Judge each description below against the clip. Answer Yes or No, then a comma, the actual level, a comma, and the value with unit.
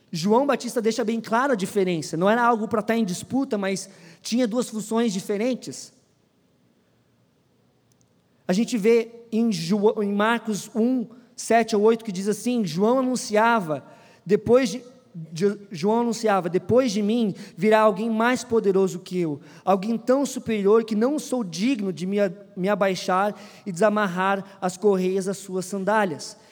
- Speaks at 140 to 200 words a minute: Yes, average, 145 wpm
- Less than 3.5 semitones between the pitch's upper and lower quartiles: Yes, average, 3.1 semitones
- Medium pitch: No, high, 215 Hz